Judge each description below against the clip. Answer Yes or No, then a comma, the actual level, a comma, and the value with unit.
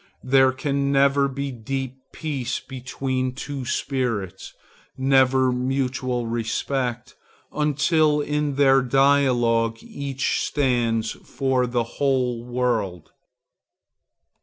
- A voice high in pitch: No, low, 130 Hz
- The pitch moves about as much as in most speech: No, narrow, 2.1 semitones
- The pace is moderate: No, slow, 90 wpm